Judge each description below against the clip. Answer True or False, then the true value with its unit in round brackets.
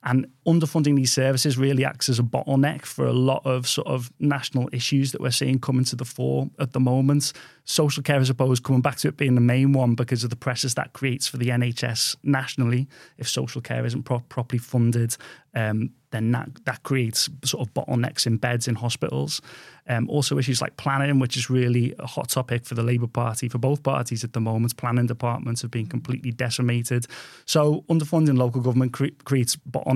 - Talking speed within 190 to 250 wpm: True (205 wpm)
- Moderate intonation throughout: False (2.1 semitones)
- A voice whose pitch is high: False (130 Hz)